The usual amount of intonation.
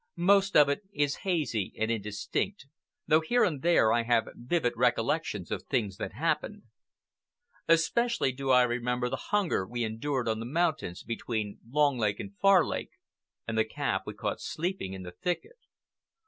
No: wide, 7.4 semitones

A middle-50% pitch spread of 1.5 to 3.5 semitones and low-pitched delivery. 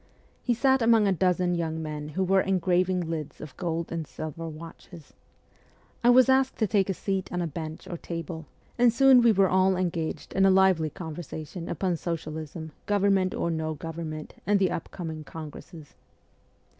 No: average, 3.2 semitones; medium, 175 Hz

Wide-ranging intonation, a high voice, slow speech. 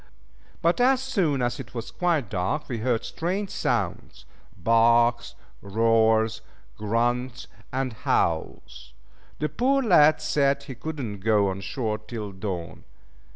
No: wide, 5.8 semitones; low, 120 Hz; slow, 130 wpm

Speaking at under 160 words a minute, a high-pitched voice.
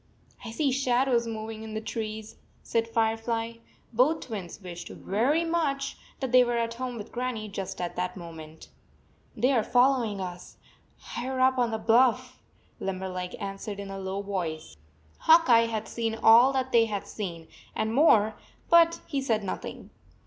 No: average, 165 wpm; high, 225 Hz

